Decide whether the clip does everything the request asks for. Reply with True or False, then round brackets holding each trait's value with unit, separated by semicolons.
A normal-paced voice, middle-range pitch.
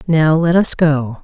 True (195 wpm; 155 Hz)